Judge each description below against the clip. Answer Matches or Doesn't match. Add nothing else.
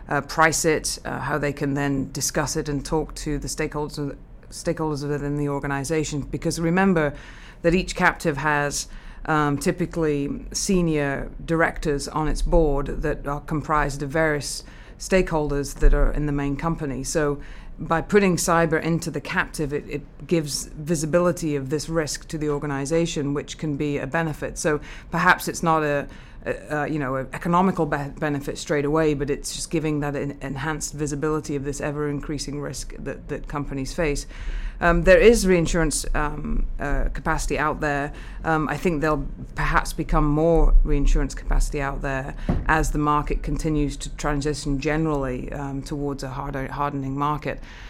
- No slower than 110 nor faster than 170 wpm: Matches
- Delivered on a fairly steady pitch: Matches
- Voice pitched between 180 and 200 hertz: Doesn't match